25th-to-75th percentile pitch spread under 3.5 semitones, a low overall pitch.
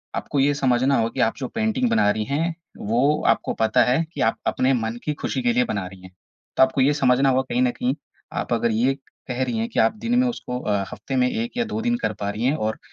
No: average, 4.7 semitones; low, 130 Hz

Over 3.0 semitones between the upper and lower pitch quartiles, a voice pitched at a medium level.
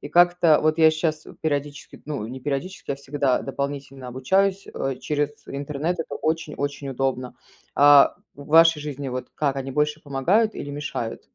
No: narrow, 2.4 semitones; medium, 145 Hz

